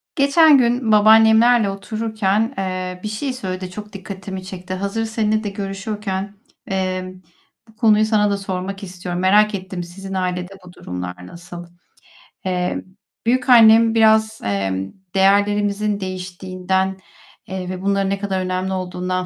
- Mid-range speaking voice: No, high, 195 Hz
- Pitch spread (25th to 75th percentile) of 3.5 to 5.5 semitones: No, average, 2.7 semitones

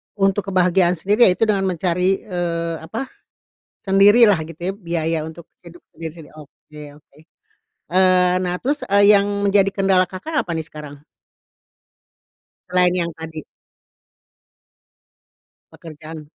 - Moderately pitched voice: Yes, medium, 180 Hz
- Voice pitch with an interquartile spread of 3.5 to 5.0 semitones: No, average, 3.1 semitones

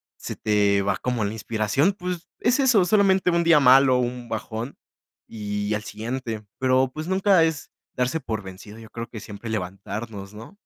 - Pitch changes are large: Yes, wide, 7.3 semitones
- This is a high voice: No, low, 120 Hz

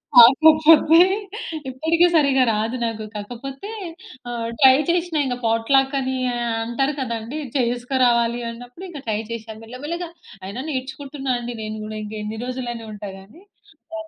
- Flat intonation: No, average, 3.6 semitones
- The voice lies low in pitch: No, very high, 250 Hz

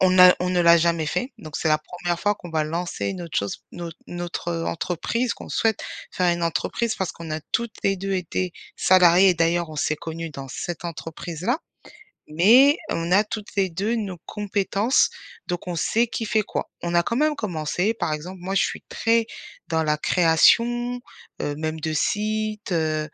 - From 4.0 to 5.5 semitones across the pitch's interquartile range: Yes, average, 4.3 semitones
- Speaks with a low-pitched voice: No, medium, 175 Hz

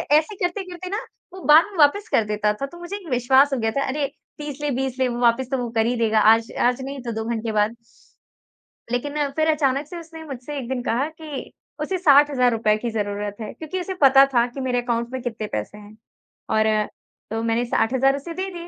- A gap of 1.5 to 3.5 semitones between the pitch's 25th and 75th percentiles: No, average, 4.7 semitones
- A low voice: No, very high, 260 Hz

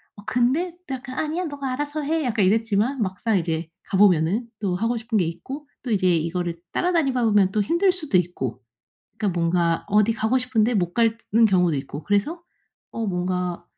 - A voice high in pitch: Yes, high, 215 Hz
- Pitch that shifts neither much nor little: No, wide, 6.1 semitones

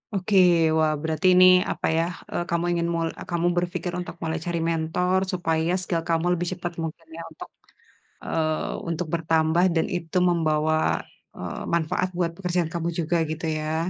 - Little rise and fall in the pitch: Yes, narrow, 1.6 semitones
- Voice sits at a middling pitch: Yes, medium, 165 Hz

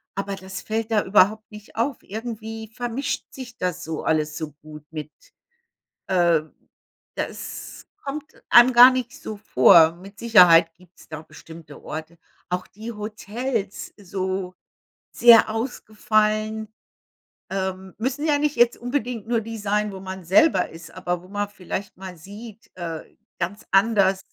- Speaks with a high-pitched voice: Yes, high, 205 Hz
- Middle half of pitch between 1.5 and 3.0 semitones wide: No, average, 3.9 semitones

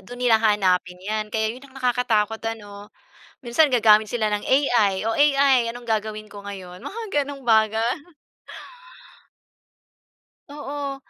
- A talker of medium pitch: No, high, 225 Hz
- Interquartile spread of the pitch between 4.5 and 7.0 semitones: No, average, 3.4 semitones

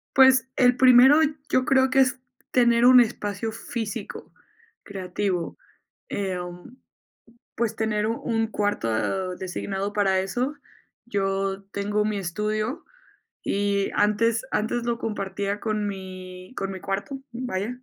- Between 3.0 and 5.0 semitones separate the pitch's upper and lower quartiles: Yes, average, 3.6 semitones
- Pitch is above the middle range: Yes, high, 210 Hz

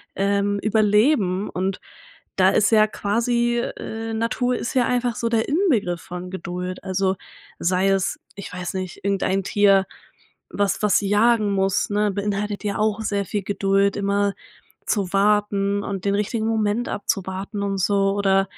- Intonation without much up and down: Yes, narrow, 1.7 semitones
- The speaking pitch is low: No, high, 200 Hz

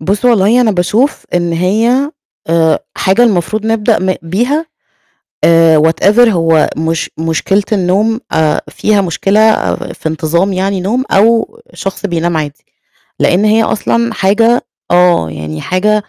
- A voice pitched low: No, high, 195 Hz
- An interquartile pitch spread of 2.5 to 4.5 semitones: No, average, 4.9 semitones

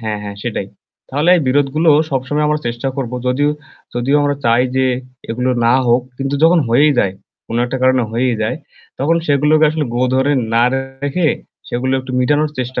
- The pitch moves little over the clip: No, average, 3.1 semitones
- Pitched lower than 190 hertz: Yes, low, 135 Hz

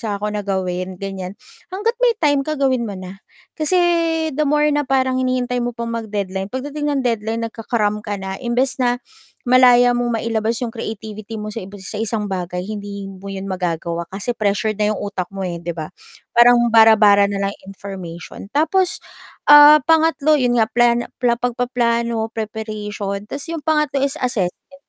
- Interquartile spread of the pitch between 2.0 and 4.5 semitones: Yes, average, 4.2 semitones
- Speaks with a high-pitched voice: Yes, high, 225 Hz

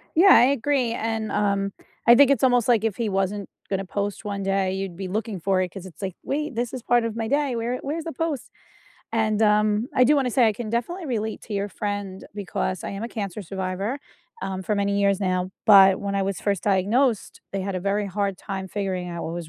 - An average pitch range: Yes, average, 3.4 semitones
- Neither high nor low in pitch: No, high, 205 Hz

